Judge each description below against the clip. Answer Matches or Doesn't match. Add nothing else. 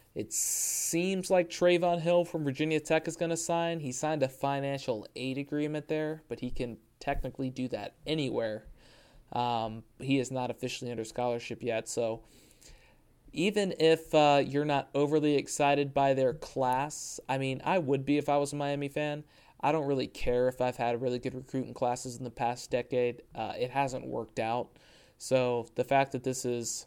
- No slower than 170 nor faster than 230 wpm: Matches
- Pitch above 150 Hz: Doesn't match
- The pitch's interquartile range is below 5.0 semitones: Matches